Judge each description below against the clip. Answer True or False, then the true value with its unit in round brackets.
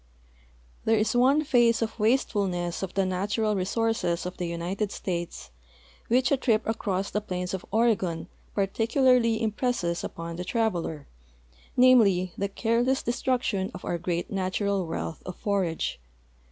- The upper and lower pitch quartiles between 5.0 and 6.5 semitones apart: False (4.2 semitones)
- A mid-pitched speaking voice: False (200 Hz)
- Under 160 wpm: True (145 wpm)